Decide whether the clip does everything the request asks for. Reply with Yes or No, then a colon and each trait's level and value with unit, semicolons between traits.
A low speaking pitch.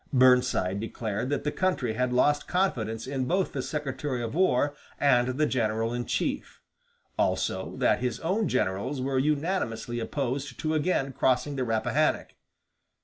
Yes: low, 130 Hz